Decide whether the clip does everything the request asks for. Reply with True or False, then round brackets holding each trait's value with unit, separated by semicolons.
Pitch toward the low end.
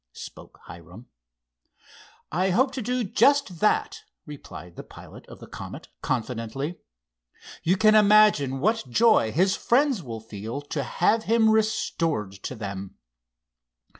False (175 Hz)